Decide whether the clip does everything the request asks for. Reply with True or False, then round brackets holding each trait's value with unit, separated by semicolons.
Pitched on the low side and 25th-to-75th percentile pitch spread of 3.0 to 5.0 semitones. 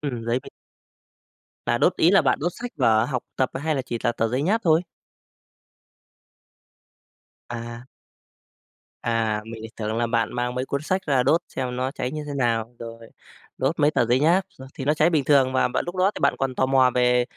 True (130 Hz; 3.9 semitones)